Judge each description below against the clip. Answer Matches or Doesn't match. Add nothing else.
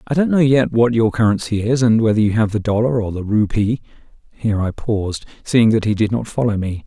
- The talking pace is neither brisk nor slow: Doesn't match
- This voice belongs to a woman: Doesn't match